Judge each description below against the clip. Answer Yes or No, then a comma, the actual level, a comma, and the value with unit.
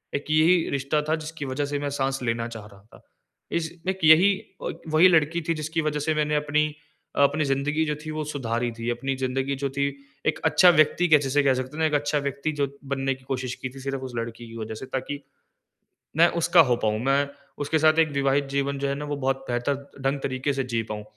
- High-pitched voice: No, medium, 140 Hz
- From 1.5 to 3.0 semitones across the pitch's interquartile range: Yes, narrow, 2.6 semitones